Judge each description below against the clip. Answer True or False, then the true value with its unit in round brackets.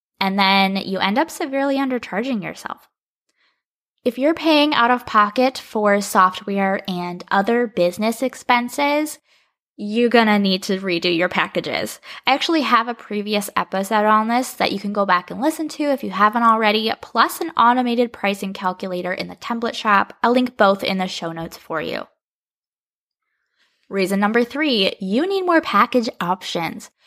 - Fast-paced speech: False (160 wpm)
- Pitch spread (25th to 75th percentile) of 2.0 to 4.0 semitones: False (4.8 semitones)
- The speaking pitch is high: True (220 Hz)